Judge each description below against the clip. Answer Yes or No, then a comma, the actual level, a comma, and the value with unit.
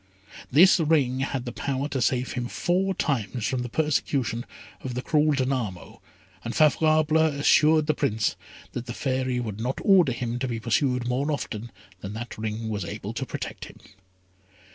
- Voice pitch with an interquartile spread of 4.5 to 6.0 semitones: No, average, 4.1 semitones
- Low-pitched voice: Yes, low, 130 Hz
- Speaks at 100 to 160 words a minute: No, average, 170 wpm